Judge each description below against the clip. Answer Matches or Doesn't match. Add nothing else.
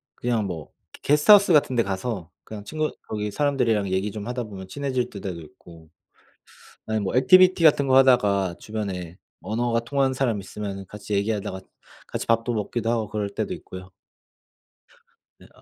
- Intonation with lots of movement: Doesn't match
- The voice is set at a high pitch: Doesn't match